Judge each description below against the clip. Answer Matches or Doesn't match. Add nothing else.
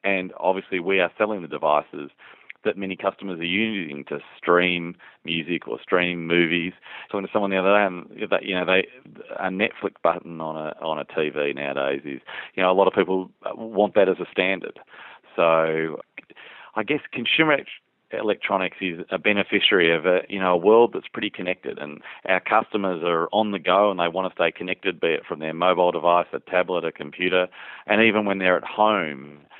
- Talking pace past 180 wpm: Matches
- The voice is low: Matches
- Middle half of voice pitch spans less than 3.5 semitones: Matches